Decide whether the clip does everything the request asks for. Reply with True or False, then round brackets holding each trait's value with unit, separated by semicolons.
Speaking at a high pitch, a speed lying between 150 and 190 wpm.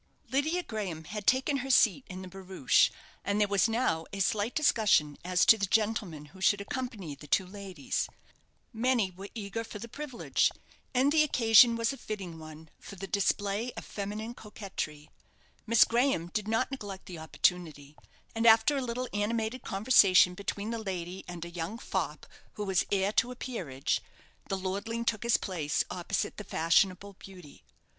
True (205 Hz; 170 wpm)